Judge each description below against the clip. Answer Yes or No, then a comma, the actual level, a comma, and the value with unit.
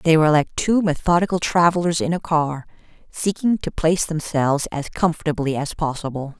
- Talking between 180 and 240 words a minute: No, average, 160 wpm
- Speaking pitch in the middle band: Yes, medium, 160 Hz